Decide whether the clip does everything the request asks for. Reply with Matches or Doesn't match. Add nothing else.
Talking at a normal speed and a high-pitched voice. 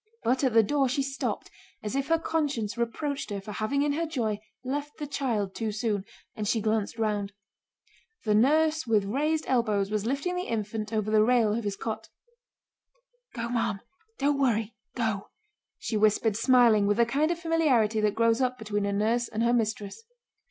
Matches